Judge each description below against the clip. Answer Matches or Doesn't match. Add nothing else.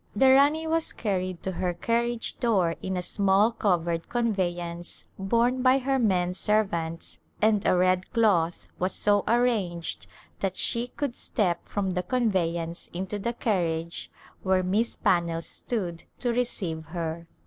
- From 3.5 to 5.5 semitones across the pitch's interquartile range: Matches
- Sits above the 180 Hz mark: Matches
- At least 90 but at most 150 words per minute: Matches